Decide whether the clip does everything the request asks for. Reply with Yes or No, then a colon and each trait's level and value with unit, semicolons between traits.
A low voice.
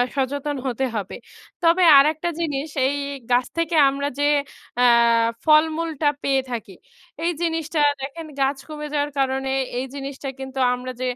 No: very high, 285 Hz